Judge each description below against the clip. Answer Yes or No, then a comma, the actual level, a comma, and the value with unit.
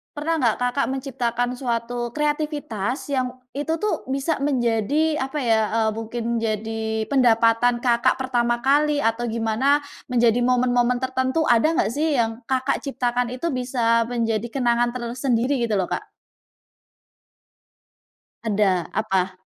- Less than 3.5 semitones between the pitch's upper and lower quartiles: Yes, average, 2.8 semitones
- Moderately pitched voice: No, high, 245 Hz